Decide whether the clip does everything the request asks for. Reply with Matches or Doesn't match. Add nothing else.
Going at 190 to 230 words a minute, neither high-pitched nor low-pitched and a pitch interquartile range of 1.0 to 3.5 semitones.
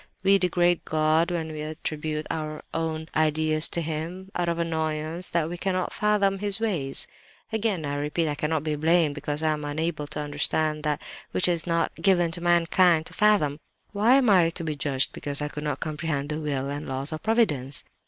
Matches